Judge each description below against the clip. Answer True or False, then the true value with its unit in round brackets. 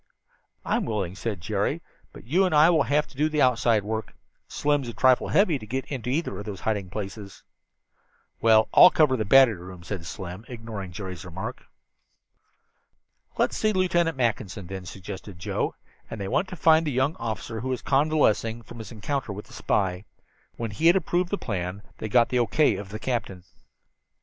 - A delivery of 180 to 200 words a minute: True (190 wpm)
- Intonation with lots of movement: True (6.2 semitones)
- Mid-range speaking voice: False (115 Hz)